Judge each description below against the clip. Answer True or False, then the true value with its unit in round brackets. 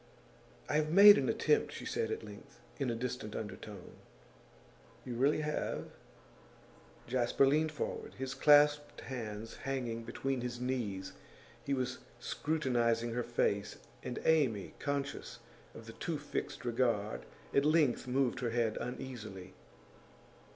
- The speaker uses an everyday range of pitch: True (3.6 semitones)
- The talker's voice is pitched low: True (125 Hz)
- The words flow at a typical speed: False (130 wpm)